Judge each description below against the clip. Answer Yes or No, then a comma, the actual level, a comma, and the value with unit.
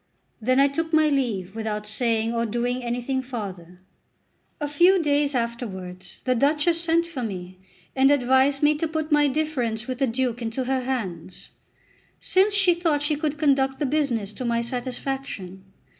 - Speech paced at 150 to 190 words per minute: Yes, average, 165 wpm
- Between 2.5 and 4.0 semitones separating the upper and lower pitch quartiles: No, average, 4.5 semitones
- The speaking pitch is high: Yes, very high, 260 Hz